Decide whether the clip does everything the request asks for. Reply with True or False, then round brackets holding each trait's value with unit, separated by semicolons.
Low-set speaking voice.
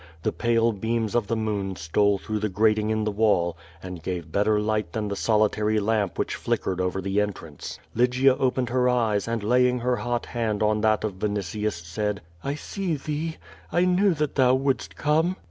True (110 Hz)